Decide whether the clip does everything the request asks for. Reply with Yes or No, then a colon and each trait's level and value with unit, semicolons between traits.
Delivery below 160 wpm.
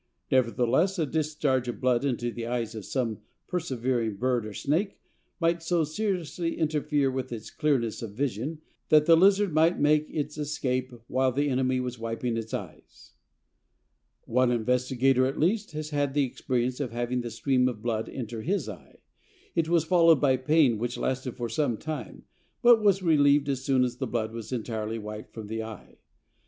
No: average, 175 wpm